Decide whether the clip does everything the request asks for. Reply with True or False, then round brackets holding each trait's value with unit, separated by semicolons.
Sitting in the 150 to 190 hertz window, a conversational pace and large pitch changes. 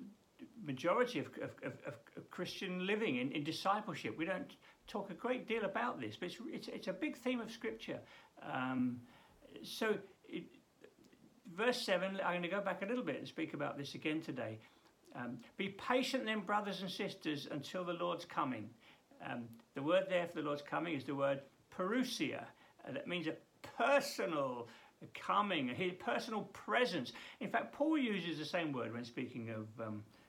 True (185 Hz; 175 wpm; 7.6 semitones)